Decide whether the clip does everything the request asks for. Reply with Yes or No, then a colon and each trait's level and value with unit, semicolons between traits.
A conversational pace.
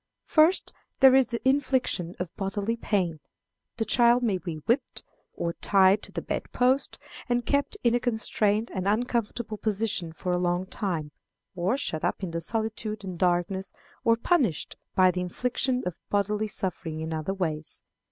Yes: average, 160 wpm